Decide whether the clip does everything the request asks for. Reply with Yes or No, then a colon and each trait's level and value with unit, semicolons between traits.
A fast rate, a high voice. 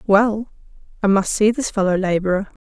No: average, 160 wpm; high, 205 Hz